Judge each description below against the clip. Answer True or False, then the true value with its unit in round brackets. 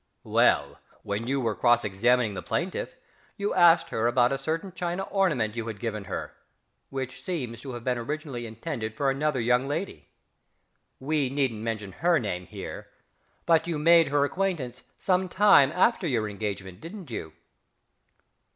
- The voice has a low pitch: True (130 Hz)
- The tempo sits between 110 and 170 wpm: True (160 wpm)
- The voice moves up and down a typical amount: False (6.4 semitones)